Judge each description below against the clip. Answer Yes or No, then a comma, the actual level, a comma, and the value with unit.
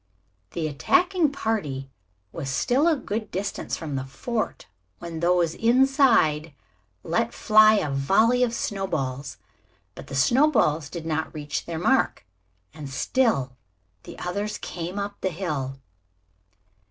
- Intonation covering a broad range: Yes, wide, 7.3 semitones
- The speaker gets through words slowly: Yes, slow, 130 wpm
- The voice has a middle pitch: Yes, medium, 175 Hz